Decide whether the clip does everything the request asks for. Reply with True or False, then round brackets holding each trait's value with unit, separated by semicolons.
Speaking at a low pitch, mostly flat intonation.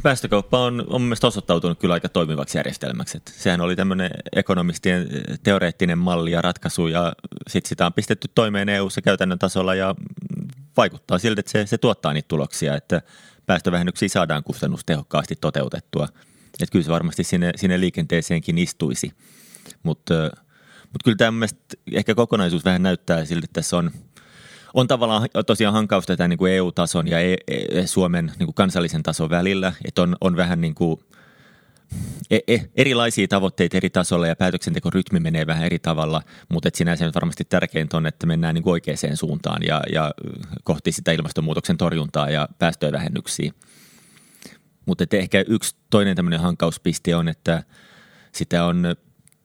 False (90 Hz; 3.4 semitones)